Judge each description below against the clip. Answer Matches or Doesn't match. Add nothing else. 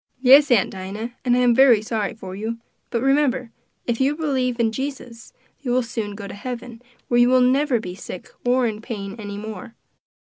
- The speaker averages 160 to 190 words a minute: Doesn't match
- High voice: Matches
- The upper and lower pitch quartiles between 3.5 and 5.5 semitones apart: Doesn't match